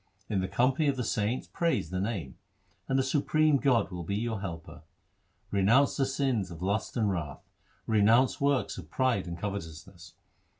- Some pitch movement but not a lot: No, wide, 6.2 semitones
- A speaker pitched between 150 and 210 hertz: No, low, 110 Hz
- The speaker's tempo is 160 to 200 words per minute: Yes, average, 170 wpm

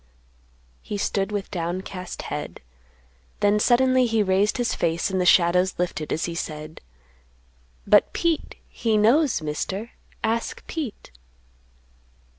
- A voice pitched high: Yes, high, 200 Hz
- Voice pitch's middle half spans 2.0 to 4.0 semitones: No, average, 4.6 semitones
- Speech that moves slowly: Yes, slow, 120 wpm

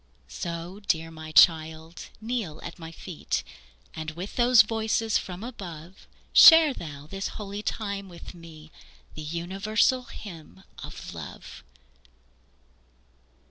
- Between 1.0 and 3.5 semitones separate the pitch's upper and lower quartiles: No, average, 4.8 semitones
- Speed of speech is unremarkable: No, slow, 115 wpm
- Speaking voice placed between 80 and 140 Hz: No, medium, 175 Hz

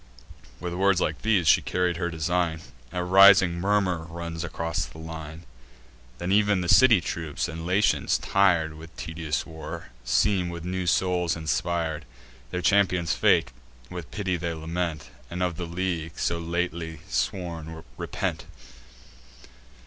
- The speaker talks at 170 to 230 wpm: No, average, 140 wpm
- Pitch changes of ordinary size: No, narrow, 1.9 semitones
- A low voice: Yes, very low, 85 Hz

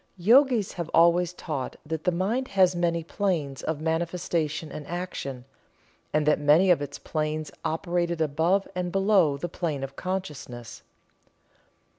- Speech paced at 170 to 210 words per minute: No, average, 145 wpm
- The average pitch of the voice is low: No, medium, 170 Hz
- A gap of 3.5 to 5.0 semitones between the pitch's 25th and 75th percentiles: No, average, 3.1 semitones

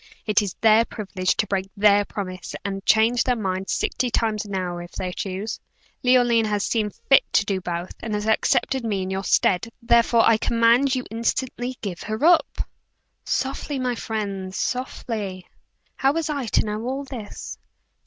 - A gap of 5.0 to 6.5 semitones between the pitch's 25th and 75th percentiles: No, average, 3.8 semitones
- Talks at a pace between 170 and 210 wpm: Yes, average, 175 wpm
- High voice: Yes, high, 220 Hz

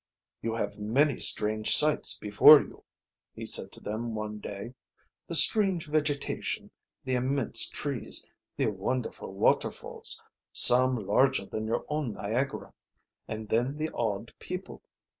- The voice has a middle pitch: No, low, 120 Hz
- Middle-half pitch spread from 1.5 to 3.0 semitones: No, average, 4.9 semitones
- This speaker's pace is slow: Yes, slow, 130 wpm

